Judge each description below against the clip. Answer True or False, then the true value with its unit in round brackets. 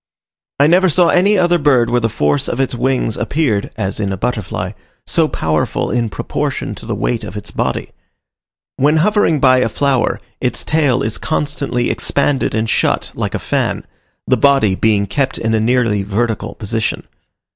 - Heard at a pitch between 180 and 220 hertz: False (125 Hz)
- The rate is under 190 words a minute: True (175 wpm)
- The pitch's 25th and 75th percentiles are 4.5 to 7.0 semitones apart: True (5.0 semitones)